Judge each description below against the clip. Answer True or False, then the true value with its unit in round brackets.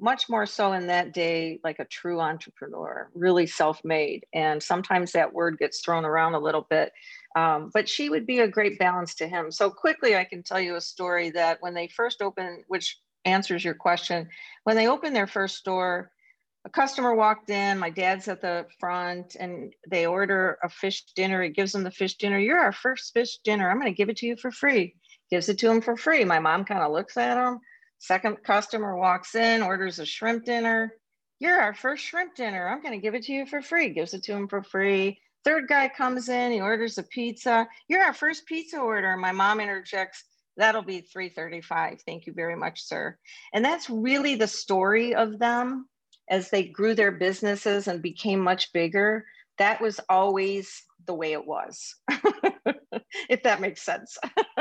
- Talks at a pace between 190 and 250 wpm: True (200 wpm)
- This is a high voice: True (200 Hz)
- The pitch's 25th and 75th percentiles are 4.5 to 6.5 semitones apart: True (4.8 semitones)